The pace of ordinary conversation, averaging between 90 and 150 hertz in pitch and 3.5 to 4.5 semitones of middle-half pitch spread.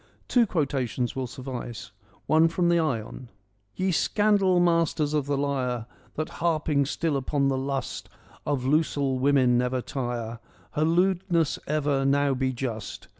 Yes: average, 150 wpm; medium, 140 Hz; average, 4.2 semitones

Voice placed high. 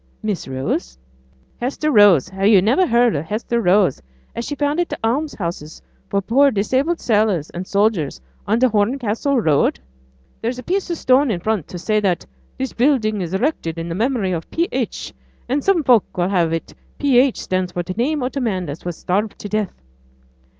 Yes: high, 215 Hz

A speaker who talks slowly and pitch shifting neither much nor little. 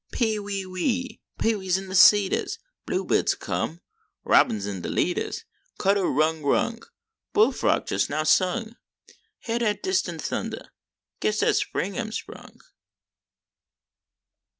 Yes: slow, 125 wpm; average, 4.2 semitones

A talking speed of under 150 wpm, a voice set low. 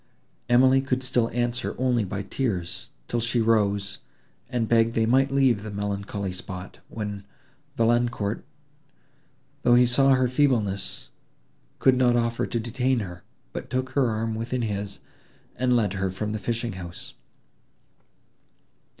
Yes: average, 140 wpm; low, 115 Hz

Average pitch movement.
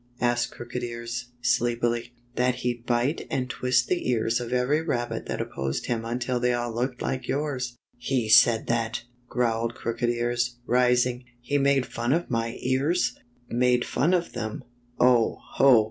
No: narrow, 1.1 semitones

